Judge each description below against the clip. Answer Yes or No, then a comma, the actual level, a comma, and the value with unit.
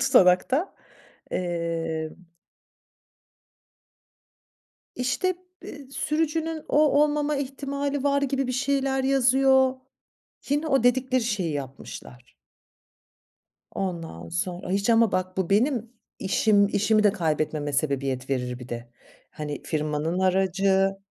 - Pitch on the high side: Yes, high, 205 Hz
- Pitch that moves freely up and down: Yes, wide, 8.7 semitones